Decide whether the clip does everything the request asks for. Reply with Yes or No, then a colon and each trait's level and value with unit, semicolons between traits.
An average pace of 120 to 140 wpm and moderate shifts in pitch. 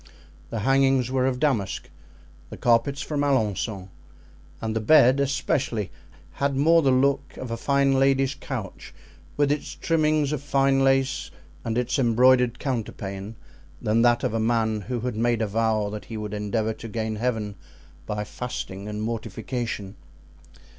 No: average, 155 wpm; average, 3.7 semitones